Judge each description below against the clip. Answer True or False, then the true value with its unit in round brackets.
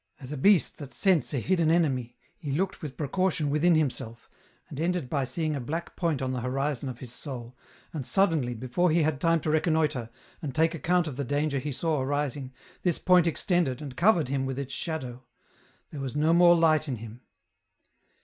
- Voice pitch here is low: False (150 Hz)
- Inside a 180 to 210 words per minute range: True (195 wpm)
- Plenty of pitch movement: False (4.1 semitones)